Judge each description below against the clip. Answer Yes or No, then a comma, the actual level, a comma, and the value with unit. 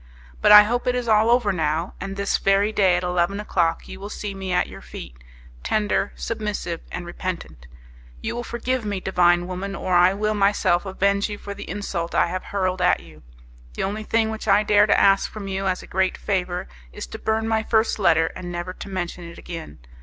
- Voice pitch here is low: No, high, 195 Hz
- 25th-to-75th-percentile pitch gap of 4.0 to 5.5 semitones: No, average, 2.9 semitones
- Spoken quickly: Yes, fast, 215 wpm